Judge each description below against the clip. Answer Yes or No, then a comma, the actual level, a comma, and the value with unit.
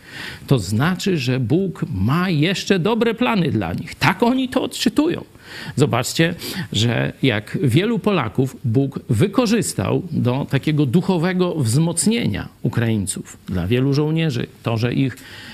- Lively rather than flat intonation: Yes, wide, 7.0 semitones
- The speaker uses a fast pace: No, average, 125 wpm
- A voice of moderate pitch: Yes, medium, 150 Hz